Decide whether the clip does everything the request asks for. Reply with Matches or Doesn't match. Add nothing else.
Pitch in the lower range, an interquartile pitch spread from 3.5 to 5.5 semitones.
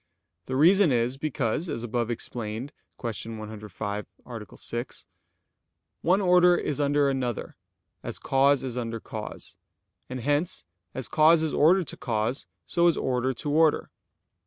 Matches